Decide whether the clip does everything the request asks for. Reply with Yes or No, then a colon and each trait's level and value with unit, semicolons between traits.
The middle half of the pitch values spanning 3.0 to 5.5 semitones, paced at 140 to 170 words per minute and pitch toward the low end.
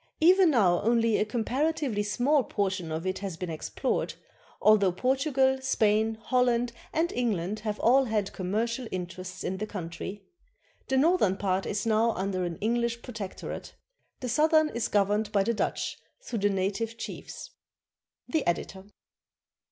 No: average, 4.4 semitones; average, 150 wpm; high, 215 Hz